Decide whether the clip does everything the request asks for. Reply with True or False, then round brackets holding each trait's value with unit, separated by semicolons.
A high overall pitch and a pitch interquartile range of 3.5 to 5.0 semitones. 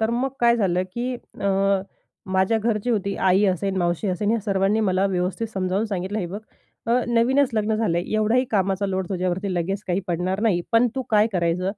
False (195 Hz; 3.1 semitones)